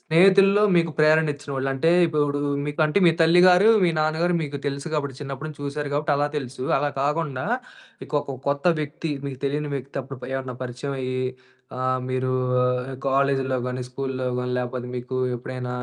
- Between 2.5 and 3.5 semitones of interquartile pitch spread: Yes, average, 2.9 semitones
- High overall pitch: No, medium, 140 Hz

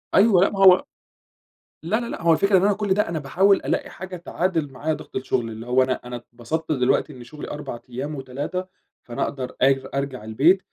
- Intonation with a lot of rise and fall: Yes, wide, 6.2 semitones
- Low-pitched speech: No, medium, 150 Hz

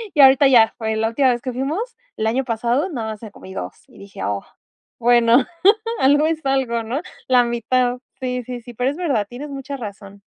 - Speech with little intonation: No, average, 3.3 semitones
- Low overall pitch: No, high, 245 Hz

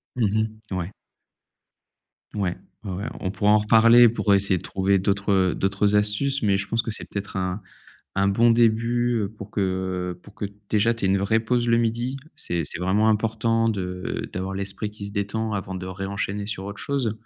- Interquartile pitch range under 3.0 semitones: Yes, narrow, 2.6 semitones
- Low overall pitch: Yes, low, 105 Hz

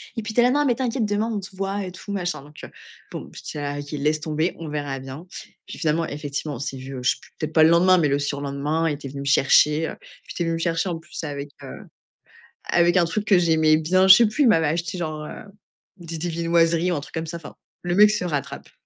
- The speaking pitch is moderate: Yes, medium, 165 Hz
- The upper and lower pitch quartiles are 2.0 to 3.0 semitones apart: No, average, 3.7 semitones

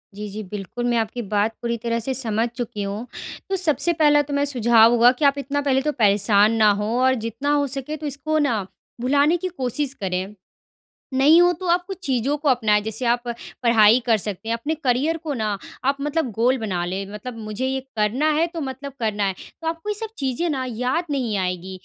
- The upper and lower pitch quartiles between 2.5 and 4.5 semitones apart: No, average, 4.9 semitones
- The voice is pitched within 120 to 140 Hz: No, very high, 250 Hz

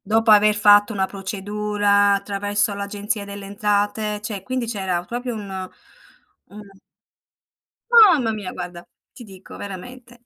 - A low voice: No, high, 205 Hz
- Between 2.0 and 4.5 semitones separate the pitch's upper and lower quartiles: No, narrow, 1.6 semitones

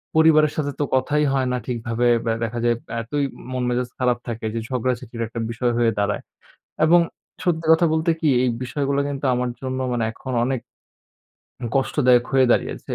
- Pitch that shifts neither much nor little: Yes, average, 3.2 semitones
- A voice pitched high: No, low, 130 Hz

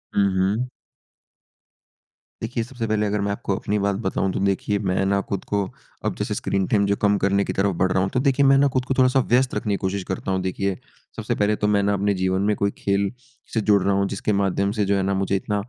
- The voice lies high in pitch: No, low, 100 Hz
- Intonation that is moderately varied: No, narrow, 1.3 semitones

